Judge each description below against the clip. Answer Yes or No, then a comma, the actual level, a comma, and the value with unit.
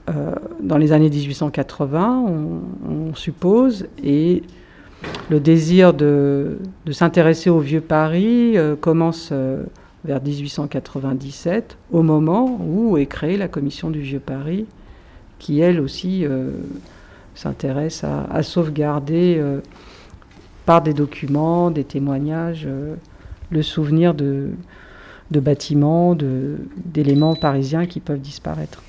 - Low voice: No, medium, 150 Hz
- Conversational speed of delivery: No, slow, 120 wpm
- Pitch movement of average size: Yes, average, 3.3 semitones